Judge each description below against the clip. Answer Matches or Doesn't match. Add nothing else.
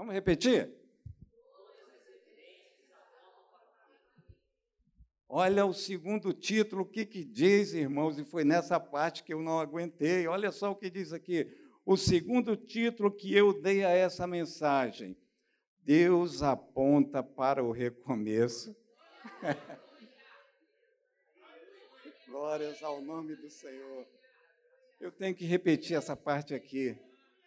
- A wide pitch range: Matches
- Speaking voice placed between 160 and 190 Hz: Matches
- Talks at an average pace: Doesn't match